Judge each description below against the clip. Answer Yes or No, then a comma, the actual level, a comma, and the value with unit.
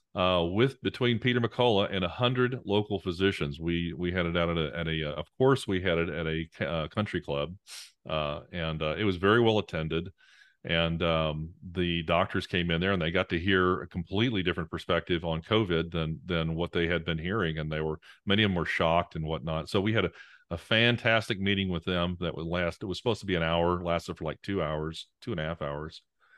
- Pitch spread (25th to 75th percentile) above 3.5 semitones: No, average, 3.2 semitones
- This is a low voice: Yes, very low, 85 Hz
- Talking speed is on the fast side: Yes, fast, 230 wpm